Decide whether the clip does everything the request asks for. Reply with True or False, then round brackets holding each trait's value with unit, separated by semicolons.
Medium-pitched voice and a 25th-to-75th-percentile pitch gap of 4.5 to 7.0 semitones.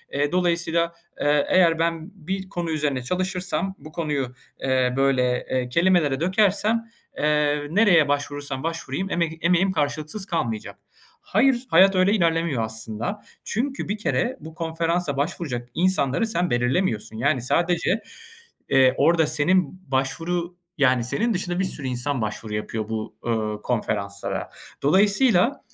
True (160 Hz; 5.6 semitones)